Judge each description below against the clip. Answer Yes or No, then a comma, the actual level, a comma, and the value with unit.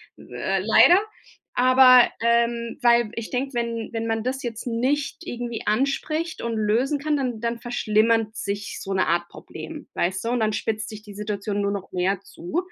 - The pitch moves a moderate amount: Yes, average, 3.0 semitones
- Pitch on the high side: Yes, high, 230 Hz